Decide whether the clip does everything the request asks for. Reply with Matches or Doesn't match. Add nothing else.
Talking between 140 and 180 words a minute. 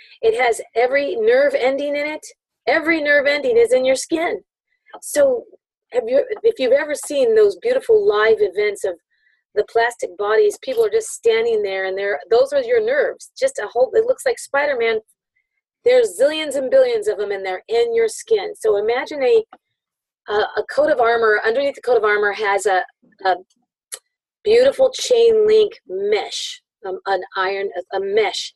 Matches